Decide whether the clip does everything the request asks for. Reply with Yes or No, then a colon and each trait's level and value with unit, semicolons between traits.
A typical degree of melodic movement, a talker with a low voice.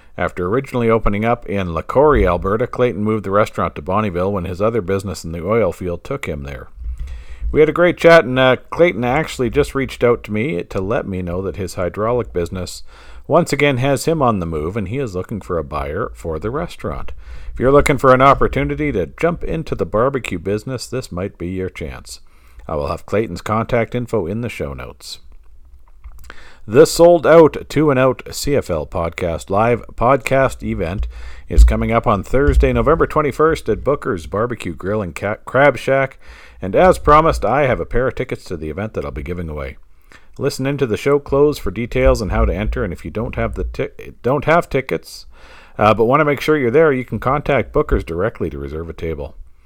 No: wide, 7.5 semitones; low, 110 Hz